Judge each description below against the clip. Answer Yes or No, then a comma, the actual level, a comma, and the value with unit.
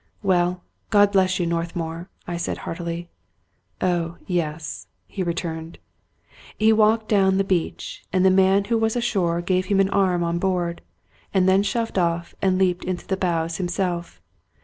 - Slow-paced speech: No, average, 170 wpm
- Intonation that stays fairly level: Yes, narrow, 2.2 semitones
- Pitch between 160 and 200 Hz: Yes, medium, 185 Hz